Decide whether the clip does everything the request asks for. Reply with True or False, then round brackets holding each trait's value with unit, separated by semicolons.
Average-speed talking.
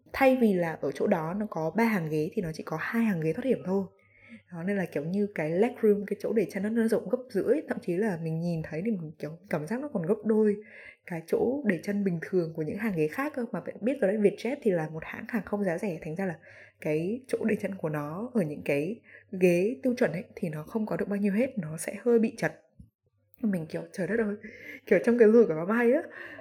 False (275 wpm)